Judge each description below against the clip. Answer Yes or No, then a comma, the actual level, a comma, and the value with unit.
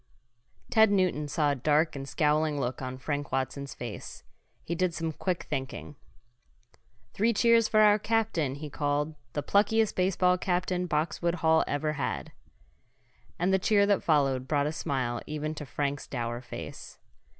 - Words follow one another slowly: No, average, 155 wpm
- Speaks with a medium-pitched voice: Yes, medium, 155 Hz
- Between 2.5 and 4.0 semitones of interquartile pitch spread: No, average, 4.5 semitones